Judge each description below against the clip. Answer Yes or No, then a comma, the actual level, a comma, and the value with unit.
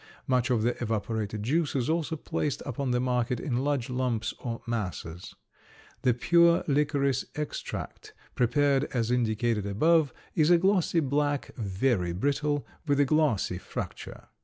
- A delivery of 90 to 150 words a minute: Yes, average, 140 wpm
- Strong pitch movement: No, average, 4.1 semitones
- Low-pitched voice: Yes, low, 130 Hz